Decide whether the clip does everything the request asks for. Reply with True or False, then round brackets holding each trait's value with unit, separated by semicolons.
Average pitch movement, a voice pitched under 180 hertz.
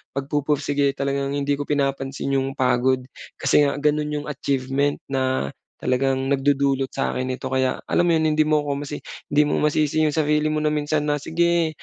False (1.9 semitones; 140 Hz)